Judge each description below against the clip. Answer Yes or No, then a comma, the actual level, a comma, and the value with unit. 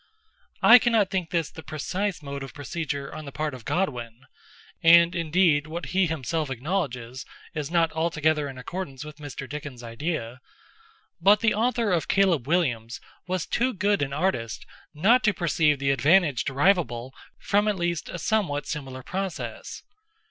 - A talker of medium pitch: Yes, medium, 160 Hz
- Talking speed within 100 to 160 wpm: Yes, average, 150 wpm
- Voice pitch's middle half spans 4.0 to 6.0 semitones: Yes, wide, 5.4 semitones